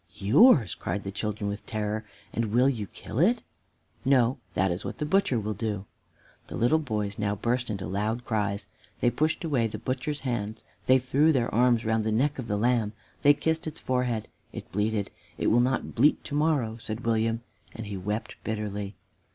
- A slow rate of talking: No, average, 190 wpm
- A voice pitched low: Yes, low, 115 Hz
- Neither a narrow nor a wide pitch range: Yes, average, 3.7 semitones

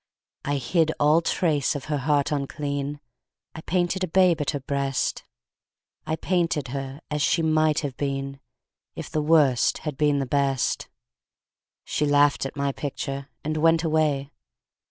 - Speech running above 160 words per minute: No, average, 155 wpm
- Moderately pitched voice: Yes, medium, 145 Hz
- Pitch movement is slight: Yes, narrow, 2.3 semitones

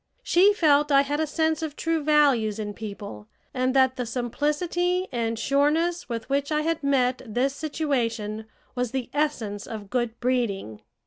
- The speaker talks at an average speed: Yes, average, 165 wpm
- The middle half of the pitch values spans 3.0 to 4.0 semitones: No, average, 4.8 semitones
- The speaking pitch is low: No, very high, 265 Hz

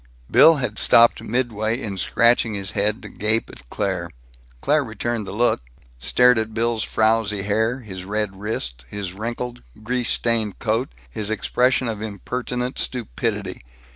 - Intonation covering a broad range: No, average, 2.7 semitones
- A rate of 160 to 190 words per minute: No, average, 145 wpm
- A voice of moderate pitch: No, low, 110 Hz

